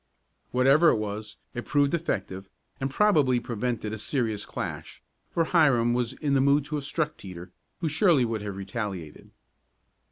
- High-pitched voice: No, low, 125 Hz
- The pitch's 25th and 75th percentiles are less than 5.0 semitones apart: No, wide, 5.5 semitones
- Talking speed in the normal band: Yes, average, 160 wpm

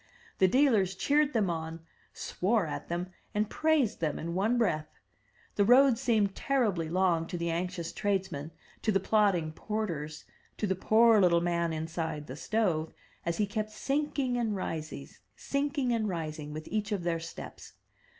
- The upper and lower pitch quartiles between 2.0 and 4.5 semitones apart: No, average, 5.1 semitones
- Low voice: No, high, 190 Hz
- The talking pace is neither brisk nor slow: Yes, average, 160 wpm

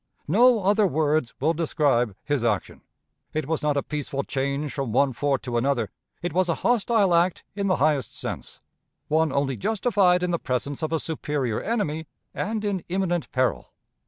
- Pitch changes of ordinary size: Yes, average, 5.0 semitones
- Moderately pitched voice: Yes, medium, 155 Hz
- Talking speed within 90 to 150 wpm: No, average, 175 wpm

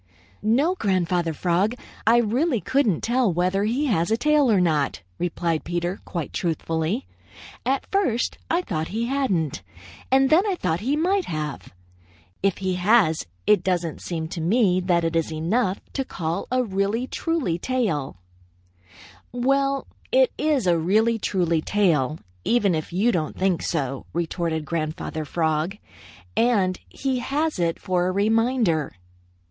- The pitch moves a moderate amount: No, wide, 6.7 semitones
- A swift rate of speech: No, average, 145 wpm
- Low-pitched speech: No, high, 190 Hz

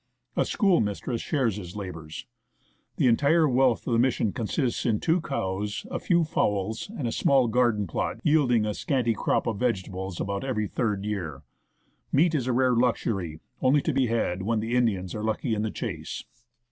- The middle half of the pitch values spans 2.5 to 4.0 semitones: No, average, 4.4 semitones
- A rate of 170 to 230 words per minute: Yes, average, 180 wpm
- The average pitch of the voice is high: No, low, 115 Hz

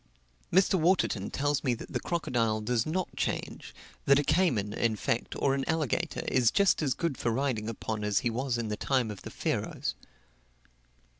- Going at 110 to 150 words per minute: No, average, 180 wpm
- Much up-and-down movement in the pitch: Yes, wide, 5.7 semitones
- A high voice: No, low, 125 Hz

